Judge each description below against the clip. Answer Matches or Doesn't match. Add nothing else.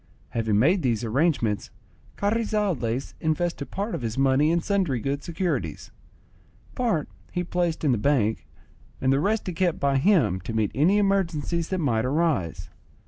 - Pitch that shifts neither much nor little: Doesn't match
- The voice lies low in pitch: Doesn't match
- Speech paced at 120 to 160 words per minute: Matches